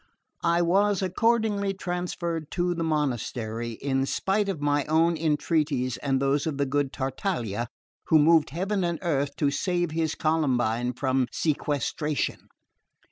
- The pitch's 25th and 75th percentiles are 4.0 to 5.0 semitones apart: Yes, average, 4.4 semitones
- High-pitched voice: No, medium, 155 Hz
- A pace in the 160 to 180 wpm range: No, slow, 135 wpm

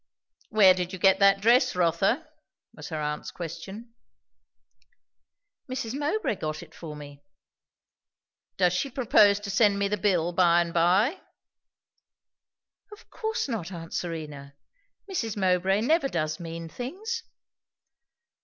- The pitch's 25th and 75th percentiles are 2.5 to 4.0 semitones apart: No, wide, 5.6 semitones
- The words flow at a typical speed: No, slow, 125 wpm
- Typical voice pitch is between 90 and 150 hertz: No, high, 190 Hz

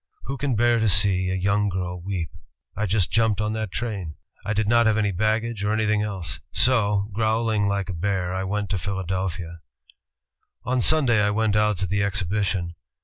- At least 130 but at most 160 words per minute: No, average, 190 wpm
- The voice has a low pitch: Yes, low, 105 Hz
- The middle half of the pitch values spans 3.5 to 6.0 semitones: No, narrow, 2.6 semitones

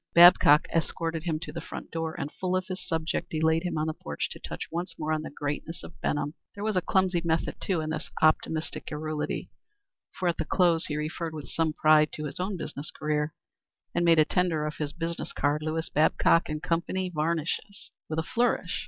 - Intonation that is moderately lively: No, narrow, 2.1 semitones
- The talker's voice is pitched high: No, medium, 160 Hz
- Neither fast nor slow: No, fast, 210 wpm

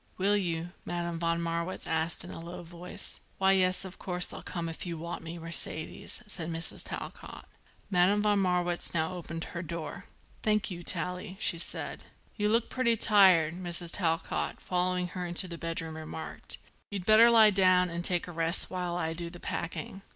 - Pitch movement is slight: Yes, narrow, 2.0 semitones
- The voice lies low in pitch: No, medium, 175 Hz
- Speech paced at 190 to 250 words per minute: No, average, 180 wpm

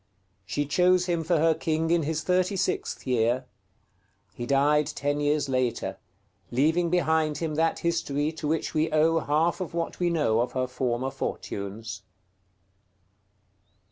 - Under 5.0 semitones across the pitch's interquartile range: Yes, average, 3.7 semitones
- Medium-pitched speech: Yes, medium, 155 Hz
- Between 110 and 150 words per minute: Yes, average, 140 wpm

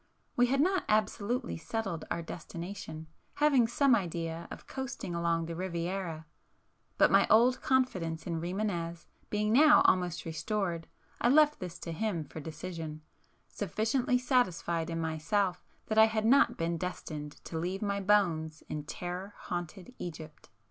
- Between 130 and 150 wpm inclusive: Yes, average, 140 wpm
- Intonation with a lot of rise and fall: No, average, 5.0 semitones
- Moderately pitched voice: Yes, medium, 180 Hz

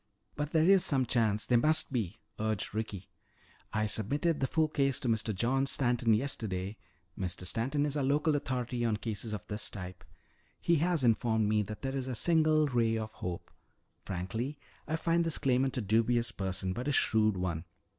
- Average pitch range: Yes, average, 4.8 semitones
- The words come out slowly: No, average, 185 wpm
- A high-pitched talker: No, low, 120 Hz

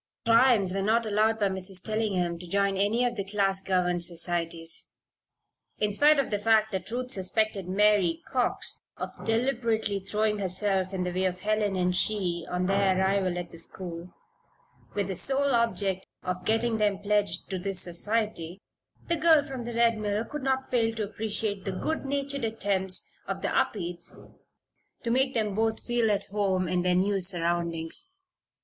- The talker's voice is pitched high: Yes, high, 200 Hz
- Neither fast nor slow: Yes, average, 170 wpm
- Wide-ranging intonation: No, average, 3.5 semitones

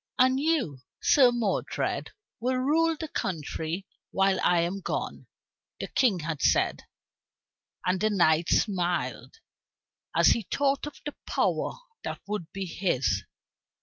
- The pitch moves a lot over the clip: Yes, wide, 6.8 semitones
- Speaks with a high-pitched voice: Yes, high, 195 Hz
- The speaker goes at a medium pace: No, slow, 130 wpm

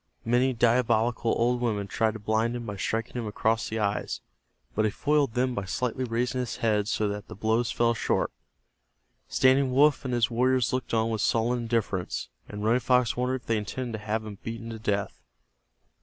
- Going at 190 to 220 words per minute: Yes, average, 195 wpm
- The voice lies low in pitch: Yes, low, 115 Hz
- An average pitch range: No, narrow, 2.2 semitones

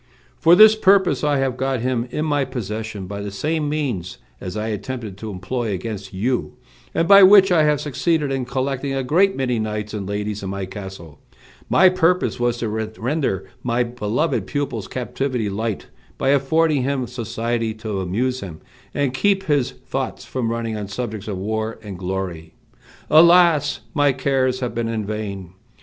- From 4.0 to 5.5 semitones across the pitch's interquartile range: Yes, average, 5.2 semitones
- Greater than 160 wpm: Yes, average, 170 wpm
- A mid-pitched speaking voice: No, low, 120 Hz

